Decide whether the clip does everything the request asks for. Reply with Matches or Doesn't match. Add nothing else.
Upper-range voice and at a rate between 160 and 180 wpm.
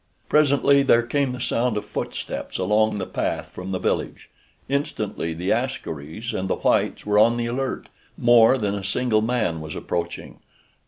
Doesn't match